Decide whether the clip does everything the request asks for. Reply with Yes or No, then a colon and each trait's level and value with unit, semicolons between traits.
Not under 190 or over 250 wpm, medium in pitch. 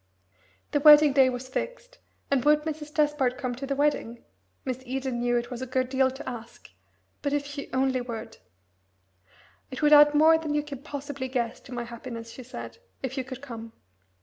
No: average, 195 wpm; very high, 265 Hz